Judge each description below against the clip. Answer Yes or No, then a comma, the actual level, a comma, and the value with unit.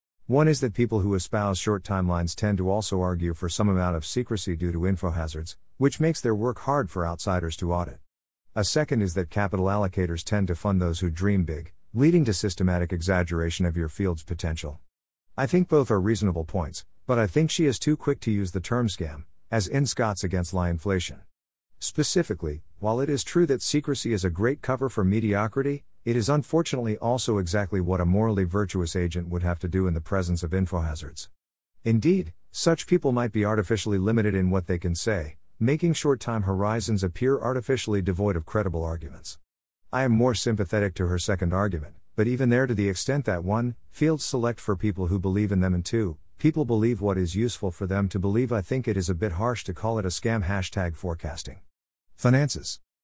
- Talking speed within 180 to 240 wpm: Yes, average, 200 wpm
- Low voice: Yes, low, 100 Hz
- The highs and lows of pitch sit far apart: No, average, 4.9 semitones